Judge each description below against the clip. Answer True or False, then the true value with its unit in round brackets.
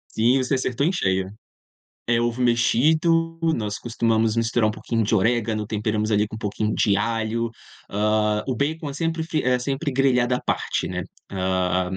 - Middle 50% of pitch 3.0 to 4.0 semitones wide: True (3.5 semitones)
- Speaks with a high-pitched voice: False (115 Hz)